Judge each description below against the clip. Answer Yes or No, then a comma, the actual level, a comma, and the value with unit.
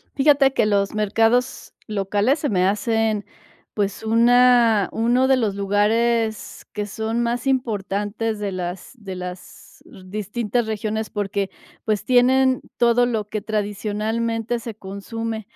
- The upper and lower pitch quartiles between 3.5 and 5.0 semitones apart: No, narrow, 2.6 semitones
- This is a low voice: No, high, 220 Hz